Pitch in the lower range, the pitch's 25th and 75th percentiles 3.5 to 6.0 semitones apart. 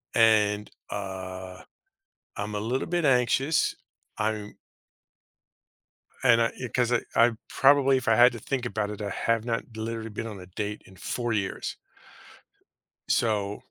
No: low, 110 Hz; average, 2.9 semitones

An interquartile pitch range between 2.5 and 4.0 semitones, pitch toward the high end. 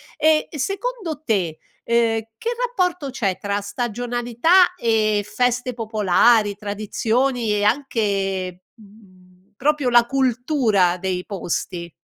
No: average, 4.5 semitones; high, 225 Hz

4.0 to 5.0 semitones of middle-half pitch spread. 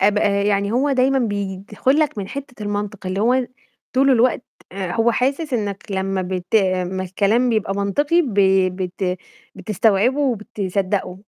Yes: average, 4.6 semitones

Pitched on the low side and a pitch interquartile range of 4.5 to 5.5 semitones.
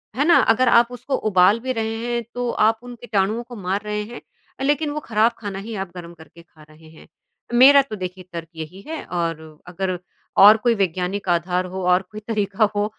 No: high, 205 Hz; average, 4.9 semitones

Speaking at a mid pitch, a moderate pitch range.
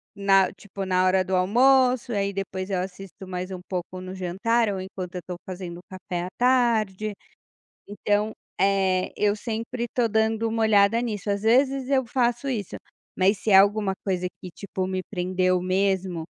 No: high, 195 Hz; average, 3.2 semitones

